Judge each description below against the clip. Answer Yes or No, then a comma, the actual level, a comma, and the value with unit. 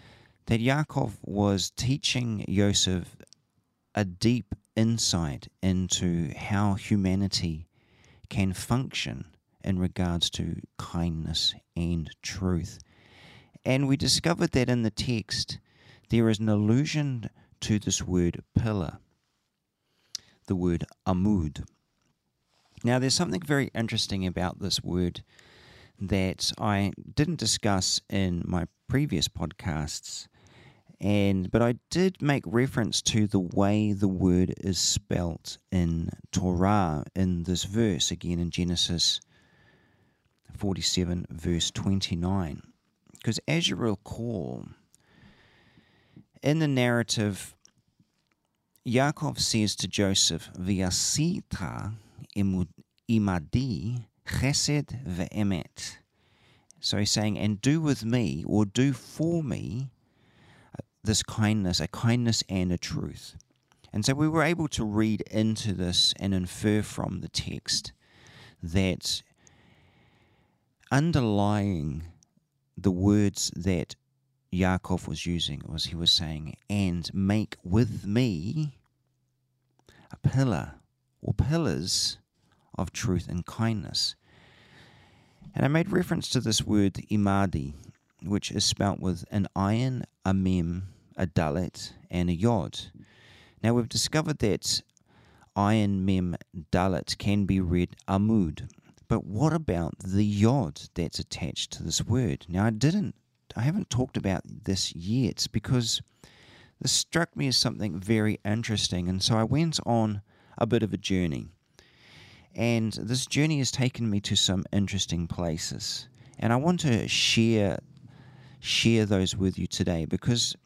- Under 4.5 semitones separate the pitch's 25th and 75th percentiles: No, average, 5.0 semitones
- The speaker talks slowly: Yes, slow, 115 wpm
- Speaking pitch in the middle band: No, low, 105 Hz